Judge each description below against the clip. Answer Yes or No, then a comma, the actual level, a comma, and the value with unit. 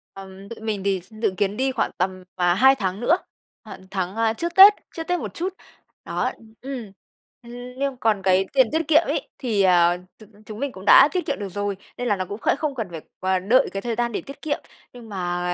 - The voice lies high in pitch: Yes, high, 215 Hz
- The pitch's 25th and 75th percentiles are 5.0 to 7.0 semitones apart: Yes, wide, 5.5 semitones